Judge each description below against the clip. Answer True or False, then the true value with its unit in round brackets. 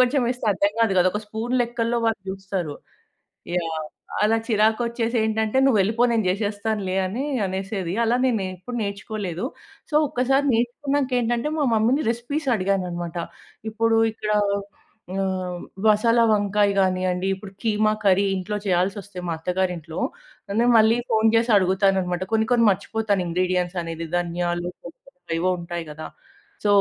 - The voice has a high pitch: True (205 Hz)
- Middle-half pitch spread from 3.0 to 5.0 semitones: True (3.7 semitones)